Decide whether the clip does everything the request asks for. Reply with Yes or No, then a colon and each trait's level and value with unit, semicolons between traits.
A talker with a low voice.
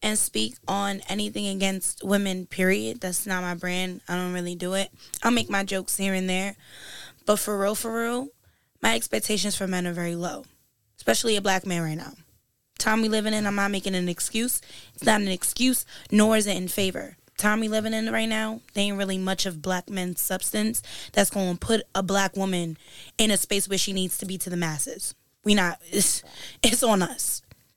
No: high, 195 Hz